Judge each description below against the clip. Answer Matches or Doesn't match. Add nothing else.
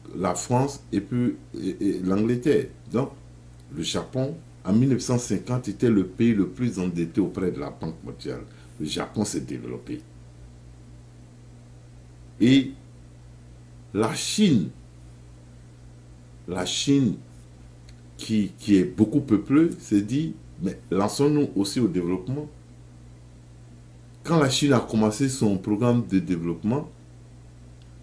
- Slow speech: Matches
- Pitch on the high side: Doesn't match